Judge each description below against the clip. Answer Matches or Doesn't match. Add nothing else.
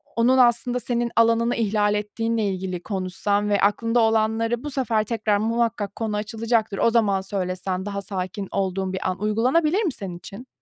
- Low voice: Doesn't match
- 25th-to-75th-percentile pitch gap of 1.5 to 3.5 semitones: Matches